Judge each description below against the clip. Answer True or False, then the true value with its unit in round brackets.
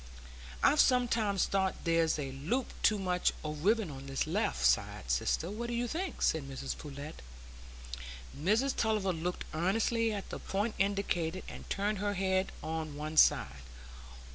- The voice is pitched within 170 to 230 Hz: True (190 Hz)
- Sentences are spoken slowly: False (155 wpm)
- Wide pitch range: True (5.7 semitones)